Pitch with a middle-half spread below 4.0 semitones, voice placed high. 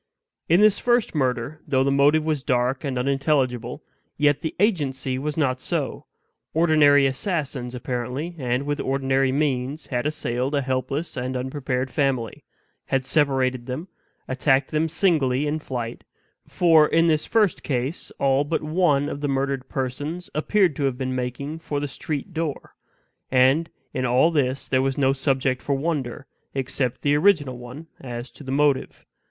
No: average, 2.9 semitones; medium, 140 Hz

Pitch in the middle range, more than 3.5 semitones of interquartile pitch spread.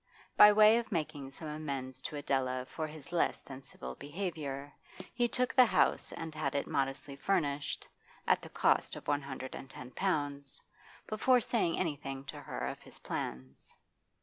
Yes: medium, 145 Hz; average, 4.4 semitones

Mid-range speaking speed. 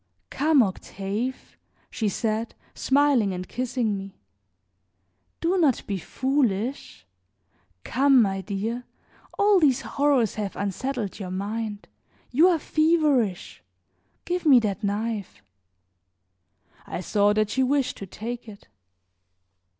No: slow, 110 wpm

